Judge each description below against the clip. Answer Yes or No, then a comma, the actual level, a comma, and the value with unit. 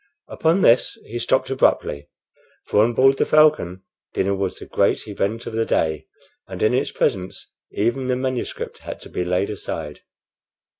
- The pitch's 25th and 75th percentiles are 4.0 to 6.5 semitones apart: Yes, wide, 5.5 semitones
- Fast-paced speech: No, average, 165 wpm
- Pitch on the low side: Yes, low, 110 Hz